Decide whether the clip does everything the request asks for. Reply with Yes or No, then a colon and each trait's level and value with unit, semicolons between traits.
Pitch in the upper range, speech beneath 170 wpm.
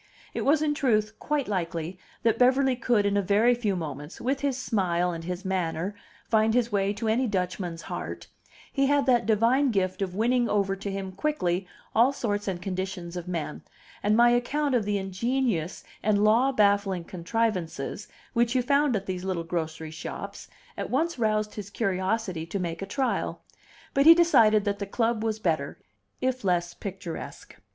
No: high, 205 Hz; average, 175 wpm